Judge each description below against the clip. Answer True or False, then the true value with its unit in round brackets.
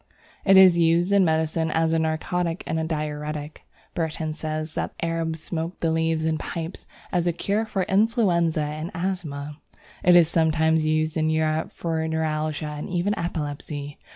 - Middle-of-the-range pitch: True (160 Hz)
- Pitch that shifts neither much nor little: False (1.7 semitones)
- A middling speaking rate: True (160 wpm)